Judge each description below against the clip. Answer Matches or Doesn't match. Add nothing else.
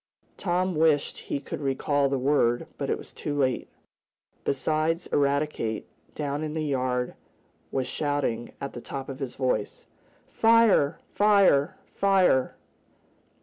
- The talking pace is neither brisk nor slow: Doesn't match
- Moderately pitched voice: Matches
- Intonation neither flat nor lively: Matches